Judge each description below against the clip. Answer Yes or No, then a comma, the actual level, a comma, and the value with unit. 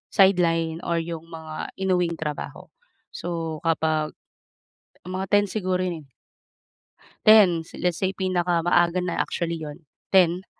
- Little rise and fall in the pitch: Yes, narrow, 2.1 semitones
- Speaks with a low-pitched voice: No, medium, 170 Hz